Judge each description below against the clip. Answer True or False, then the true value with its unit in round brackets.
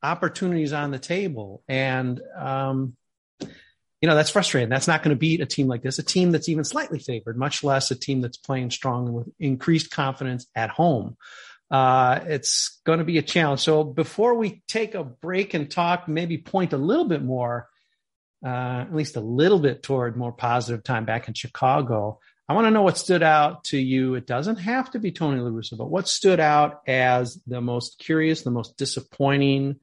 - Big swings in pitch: False (4.3 semitones)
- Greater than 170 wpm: True (195 wpm)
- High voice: False (140 Hz)